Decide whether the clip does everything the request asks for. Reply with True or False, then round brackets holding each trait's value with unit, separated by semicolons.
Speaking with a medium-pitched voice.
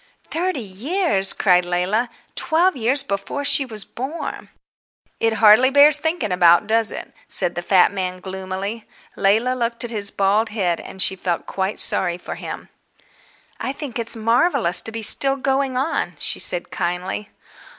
False (220 Hz)